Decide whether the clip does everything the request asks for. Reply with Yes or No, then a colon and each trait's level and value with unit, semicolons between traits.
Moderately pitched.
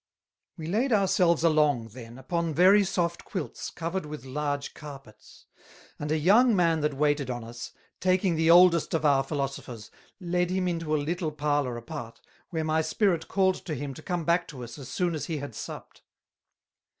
Yes: medium, 155 Hz